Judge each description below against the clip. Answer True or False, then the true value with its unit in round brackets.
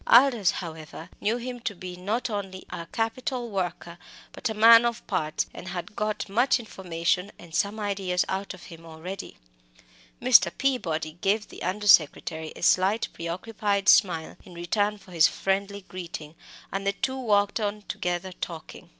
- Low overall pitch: False (195 Hz)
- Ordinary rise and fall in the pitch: True (3.6 semitones)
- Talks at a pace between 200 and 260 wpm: False (160 wpm)